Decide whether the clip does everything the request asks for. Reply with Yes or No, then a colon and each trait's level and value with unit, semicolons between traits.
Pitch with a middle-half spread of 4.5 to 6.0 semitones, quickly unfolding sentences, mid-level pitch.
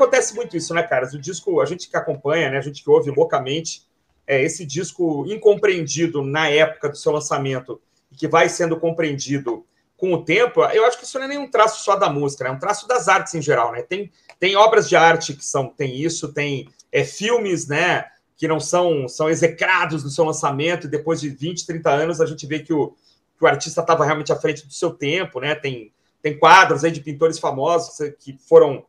No: average, 3.8 semitones; fast, 220 wpm; medium, 165 Hz